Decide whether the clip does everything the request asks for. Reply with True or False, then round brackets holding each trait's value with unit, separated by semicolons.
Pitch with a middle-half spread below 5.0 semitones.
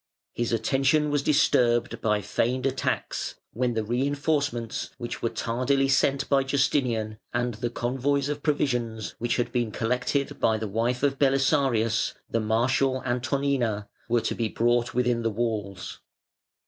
True (3.0 semitones)